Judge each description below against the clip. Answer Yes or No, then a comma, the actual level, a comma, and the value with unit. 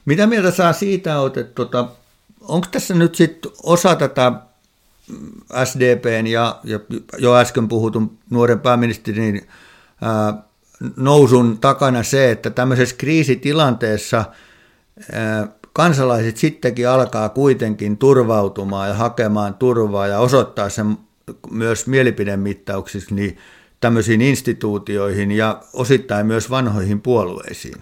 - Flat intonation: No, average, 3.6 semitones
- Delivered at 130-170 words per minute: No, average, 100 wpm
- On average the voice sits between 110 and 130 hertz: Yes, low, 120 Hz